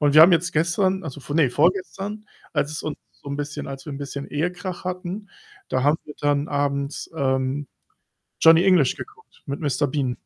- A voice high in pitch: No, medium, 150 Hz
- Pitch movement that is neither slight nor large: Yes, average, 4.1 semitones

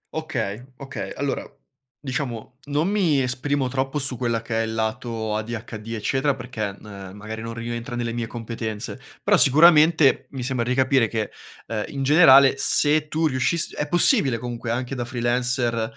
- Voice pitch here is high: No, low, 125 Hz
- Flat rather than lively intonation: No, average, 3.2 semitones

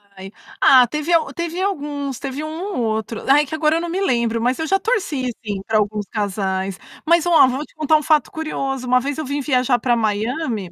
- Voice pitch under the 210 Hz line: No, very high, 270 Hz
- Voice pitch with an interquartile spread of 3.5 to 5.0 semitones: No, wide, 5.6 semitones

